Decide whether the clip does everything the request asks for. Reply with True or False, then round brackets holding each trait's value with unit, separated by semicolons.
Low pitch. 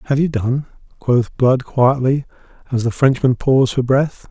True (130 Hz)